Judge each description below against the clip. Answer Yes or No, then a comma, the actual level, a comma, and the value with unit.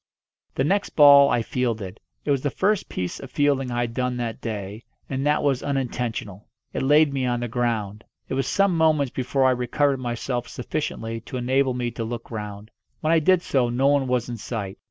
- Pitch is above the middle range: No, low, 125 Hz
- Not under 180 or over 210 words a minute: Yes, fast, 205 wpm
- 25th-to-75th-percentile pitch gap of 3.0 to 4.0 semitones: Yes, average, 3.3 semitones